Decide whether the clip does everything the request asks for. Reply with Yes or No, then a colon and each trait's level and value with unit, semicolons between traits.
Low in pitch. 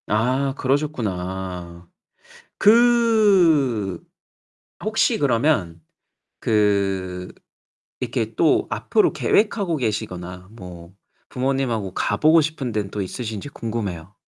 Yes: low, 110 Hz